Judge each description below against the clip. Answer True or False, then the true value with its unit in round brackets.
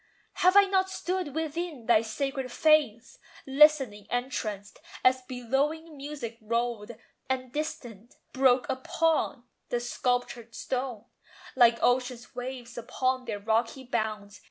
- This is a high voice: True (255 Hz)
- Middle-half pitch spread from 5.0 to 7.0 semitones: False (3.7 semitones)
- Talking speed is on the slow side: True (115 wpm)